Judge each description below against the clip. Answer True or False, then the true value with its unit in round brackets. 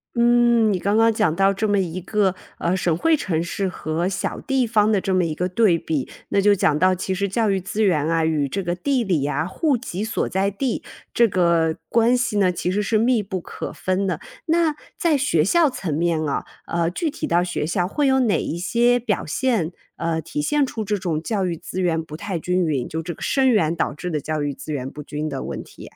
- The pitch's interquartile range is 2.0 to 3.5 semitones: False (5.2 semitones)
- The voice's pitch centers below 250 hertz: True (185 Hz)